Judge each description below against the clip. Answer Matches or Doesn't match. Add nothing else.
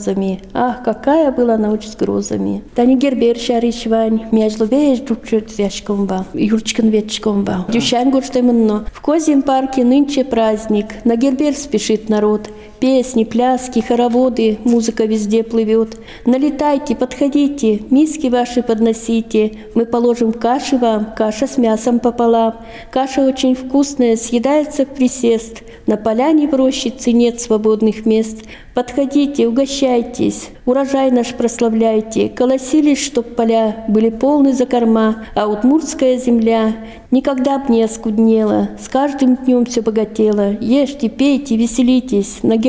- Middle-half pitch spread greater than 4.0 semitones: Doesn't match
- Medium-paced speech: Doesn't match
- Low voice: Doesn't match